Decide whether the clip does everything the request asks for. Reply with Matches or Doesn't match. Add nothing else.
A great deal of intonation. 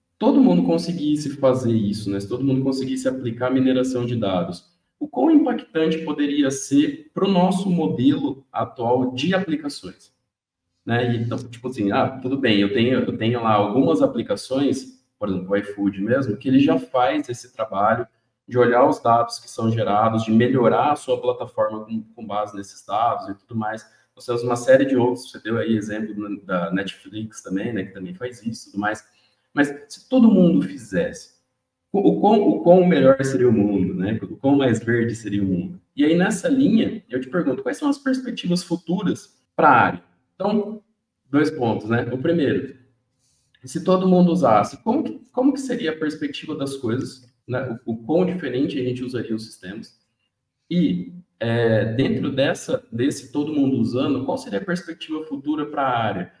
Matches